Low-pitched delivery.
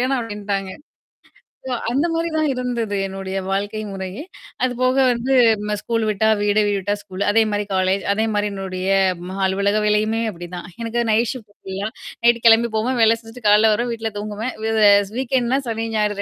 No: high, 215 Hz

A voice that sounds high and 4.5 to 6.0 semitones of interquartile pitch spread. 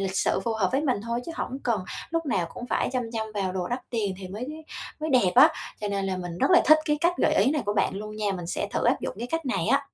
Yes: high, 220 Hz; average, 5.3 semitones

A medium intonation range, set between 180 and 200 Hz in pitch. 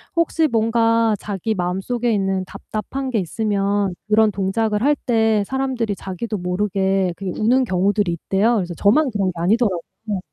No: average, 3.1 semitones; high, 210 Hz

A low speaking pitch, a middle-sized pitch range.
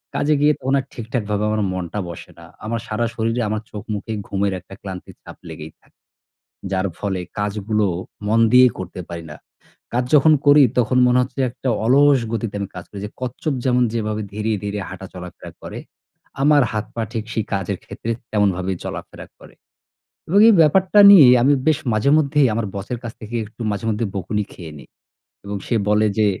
Yes: low, 110 Hz; average, 4.0 semitones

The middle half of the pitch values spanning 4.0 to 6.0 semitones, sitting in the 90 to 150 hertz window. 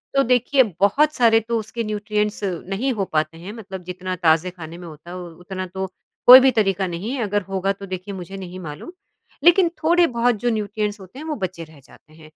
No: average, 4.4 semitones; high, 195 Hz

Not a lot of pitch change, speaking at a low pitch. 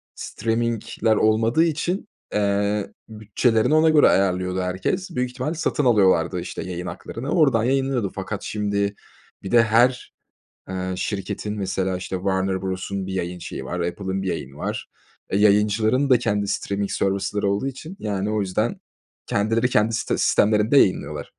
No: average, 3.7 semitones; low, 105 Hz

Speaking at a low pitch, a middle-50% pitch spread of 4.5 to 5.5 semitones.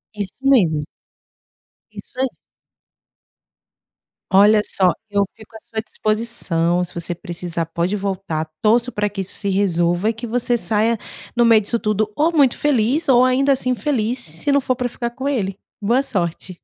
No: high, 215 Hz; average, 4.8 semitones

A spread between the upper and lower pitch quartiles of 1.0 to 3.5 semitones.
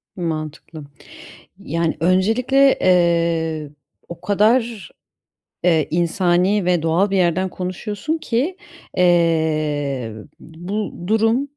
No: average, 4.3 semitones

